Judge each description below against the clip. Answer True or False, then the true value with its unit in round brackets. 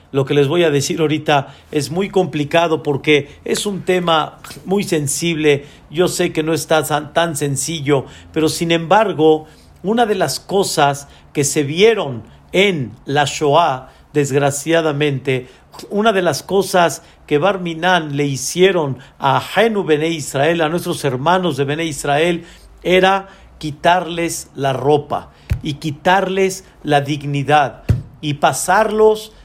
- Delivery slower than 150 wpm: True (130 wpm)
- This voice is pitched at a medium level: True (155 Hz)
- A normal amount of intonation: True (3.7 semitones)